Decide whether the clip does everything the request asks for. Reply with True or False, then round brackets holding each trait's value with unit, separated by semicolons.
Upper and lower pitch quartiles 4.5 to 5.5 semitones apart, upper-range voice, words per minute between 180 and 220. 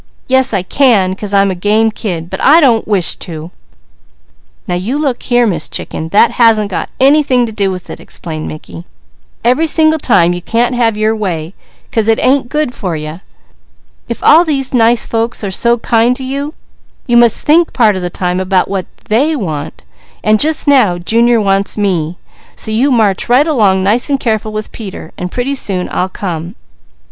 True (5.1 semitones; 220 Hz; 190 wpm)